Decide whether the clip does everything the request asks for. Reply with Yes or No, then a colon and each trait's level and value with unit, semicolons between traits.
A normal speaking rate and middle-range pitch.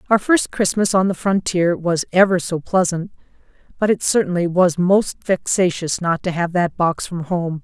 Yes: average, 180 wpm; medium, 180 Hz